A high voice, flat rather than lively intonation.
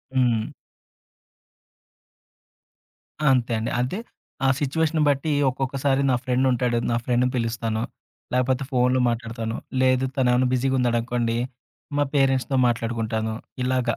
No: low, 125 Hz; narrow, 2.0 semitones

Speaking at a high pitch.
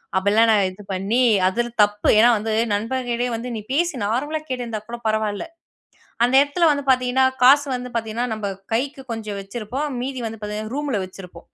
Yes: high, 230 Hz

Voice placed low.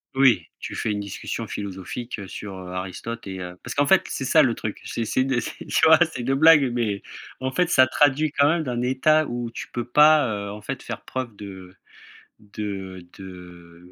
Yes: low, 115 Hz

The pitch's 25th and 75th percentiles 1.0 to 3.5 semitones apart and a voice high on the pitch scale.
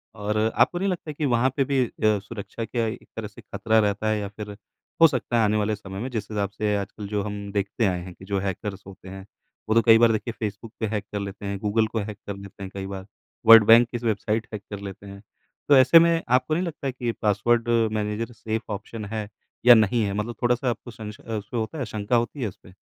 No: average, 2.7 semitones; low, 110 Hz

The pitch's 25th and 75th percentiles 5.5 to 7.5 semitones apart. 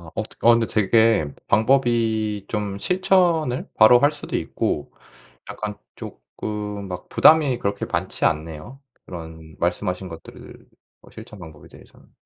No: average, 5.1 semitones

